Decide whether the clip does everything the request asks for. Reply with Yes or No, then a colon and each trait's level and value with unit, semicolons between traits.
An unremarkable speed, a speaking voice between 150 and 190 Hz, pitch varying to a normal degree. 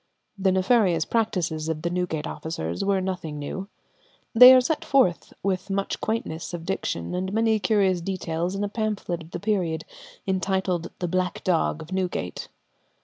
Yes: average, 160 wpm; medium, 185 Hz; average, 3.2 semitones